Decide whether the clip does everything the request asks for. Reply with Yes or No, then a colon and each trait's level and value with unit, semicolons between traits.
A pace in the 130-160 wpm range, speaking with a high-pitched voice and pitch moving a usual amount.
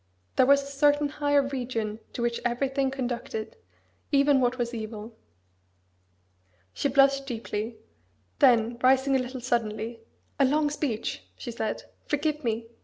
Yes: slow, 135 wpm; very high, 255 Hz; average, 3.0 semitones